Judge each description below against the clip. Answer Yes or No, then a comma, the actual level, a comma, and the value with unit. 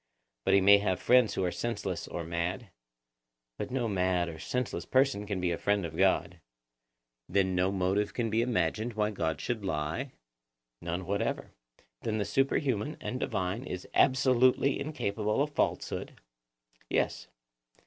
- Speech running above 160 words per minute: No, average, 150 wpm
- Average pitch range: Yes, average, 4.9 semitones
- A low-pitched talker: Yes, low, 100 Hz